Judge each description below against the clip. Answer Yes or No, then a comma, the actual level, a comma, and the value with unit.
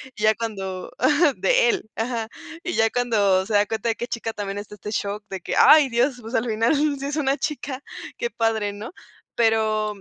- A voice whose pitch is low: No, high, 225 Hz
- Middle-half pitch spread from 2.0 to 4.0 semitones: No, average, 4.5 semitones